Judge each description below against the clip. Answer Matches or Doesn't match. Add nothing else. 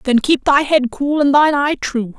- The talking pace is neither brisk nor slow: Doesn't match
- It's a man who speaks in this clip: Doesn't match